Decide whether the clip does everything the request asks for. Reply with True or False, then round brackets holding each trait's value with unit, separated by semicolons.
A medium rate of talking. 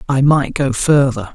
True (180 wpm)